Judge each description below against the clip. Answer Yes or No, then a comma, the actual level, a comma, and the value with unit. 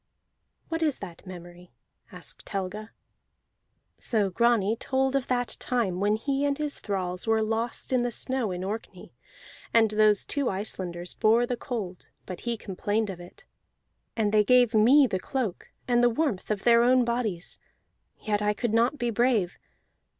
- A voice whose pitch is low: No, high, 220 Hz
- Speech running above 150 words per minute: Yes, average, 165 wpm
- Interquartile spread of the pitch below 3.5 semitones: No, average, 3.9 semitones